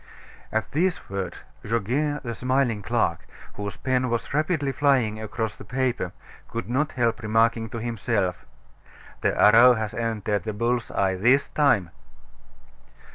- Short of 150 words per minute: Yes, slow, 135 wpm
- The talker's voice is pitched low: Yes, low, 115 Hz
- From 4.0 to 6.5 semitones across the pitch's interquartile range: No, average, 3.4 semitones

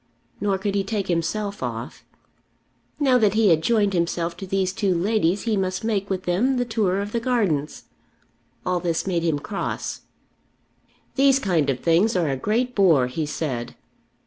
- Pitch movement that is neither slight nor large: Yes, average, 4.1 semitones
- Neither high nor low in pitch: No, high, 195 Hz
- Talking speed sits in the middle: Yes, average, 170 wpm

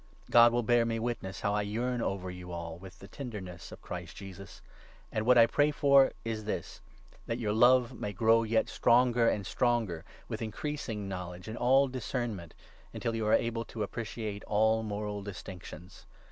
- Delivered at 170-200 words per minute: Yes, average, 190 wpm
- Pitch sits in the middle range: No, low, 110 Hz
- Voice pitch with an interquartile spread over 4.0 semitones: No, average, 3.4 semitones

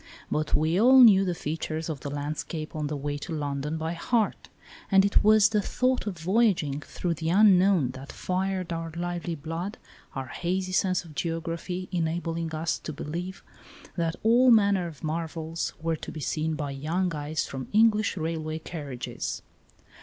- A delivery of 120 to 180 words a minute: Yes, average, 170 wpm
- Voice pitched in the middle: Yes, medium, 165 Hz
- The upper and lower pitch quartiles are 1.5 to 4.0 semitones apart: Yes, average, 3.5 semitones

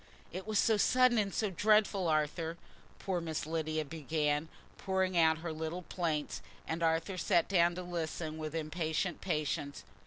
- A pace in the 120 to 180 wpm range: Yes, average, 155 wpm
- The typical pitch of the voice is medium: Yes, medium, 165 Hz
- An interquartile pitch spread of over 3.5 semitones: No, average, 2.8 semitones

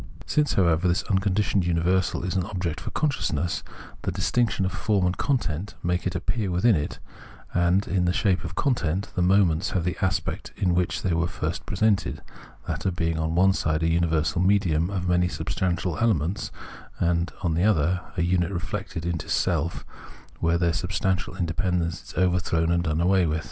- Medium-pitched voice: No, very low, 90 Hz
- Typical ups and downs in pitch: No, narrow, 2.2 semitones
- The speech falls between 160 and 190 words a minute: Yes, average, 180 wpm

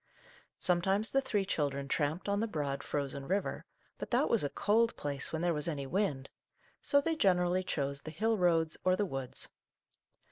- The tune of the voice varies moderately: No, wide, 6.0 semitones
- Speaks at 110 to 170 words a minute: No, average, 180 wpm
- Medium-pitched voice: Yes, medium, 175 Hz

